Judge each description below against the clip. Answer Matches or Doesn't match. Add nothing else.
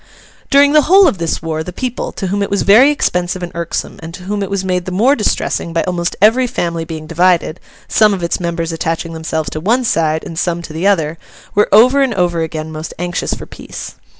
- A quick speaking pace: Matches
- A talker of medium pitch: Matches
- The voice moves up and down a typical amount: Matches